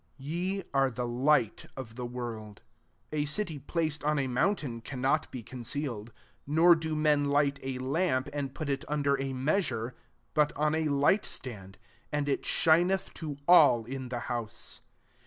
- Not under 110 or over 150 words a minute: No, average, 175 wpm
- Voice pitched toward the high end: No, medium, 140 Hz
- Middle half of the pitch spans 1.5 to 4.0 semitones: Yes, average, 3.5 semitones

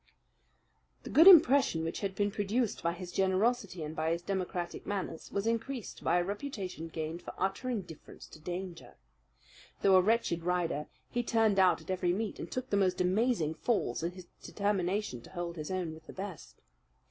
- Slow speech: No, average, 180 wpm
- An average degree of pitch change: Yes, average, 3.6 semitones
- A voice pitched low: No, medium, 185 Hz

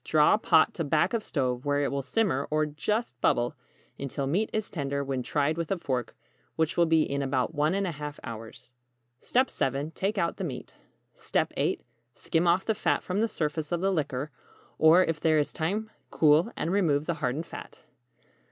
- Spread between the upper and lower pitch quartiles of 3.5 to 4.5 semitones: Yes, average, 4.0 semitones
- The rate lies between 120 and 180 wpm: No, average, 190 wpm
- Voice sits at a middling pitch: Yes, medium, 155 Hz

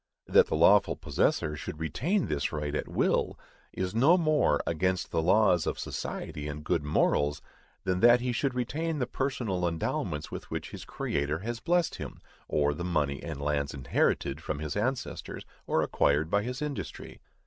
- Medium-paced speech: Yes, average, 170 wpm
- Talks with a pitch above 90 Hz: No, very low, 85 Hz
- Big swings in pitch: Yes, wide, 8.8 semitones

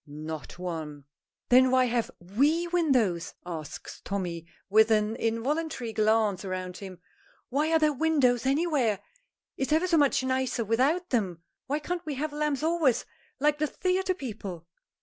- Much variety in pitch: Yes, wide, 7.5 semitones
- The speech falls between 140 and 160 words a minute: Yes, average, 150 wpm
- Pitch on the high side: Yes, very high, 250 Hz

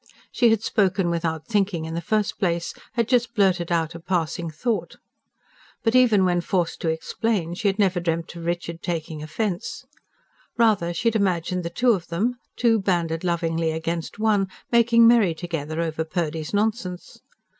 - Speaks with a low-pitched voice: No, medium, 175 Hz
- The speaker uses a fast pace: No, average, 165 wpm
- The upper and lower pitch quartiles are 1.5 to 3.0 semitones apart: No, average, 4.4 semitones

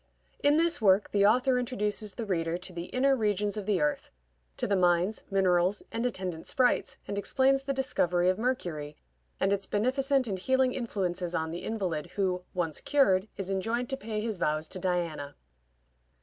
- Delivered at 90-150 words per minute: No, average, 175 wpm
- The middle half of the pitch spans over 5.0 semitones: Yes, wide, 5.4 semitones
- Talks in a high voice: Yes, high, 200 Hz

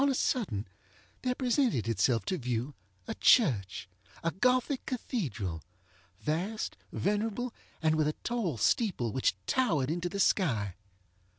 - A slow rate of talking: Yes, slow, 120 wpm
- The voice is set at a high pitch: No, medium, 155 Hz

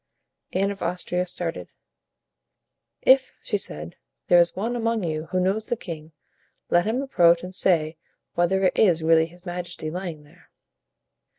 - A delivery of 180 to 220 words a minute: No, average, 155 wpm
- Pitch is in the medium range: Yes, medium, 180 Hz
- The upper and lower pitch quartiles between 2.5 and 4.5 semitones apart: Yes, average, 2.9 semitones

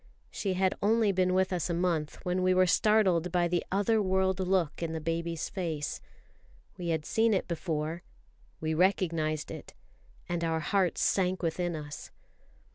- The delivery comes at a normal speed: Yes, average, 165 wpm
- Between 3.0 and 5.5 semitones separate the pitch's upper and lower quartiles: No, narrow, 2.4 semitones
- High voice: No, medium, 180 Hz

